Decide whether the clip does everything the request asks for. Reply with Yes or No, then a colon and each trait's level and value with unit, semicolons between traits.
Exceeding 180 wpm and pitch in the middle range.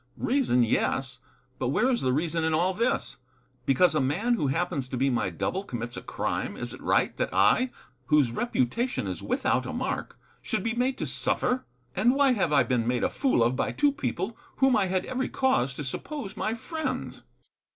Yes: average, 200 wpm; medium, 175 Hz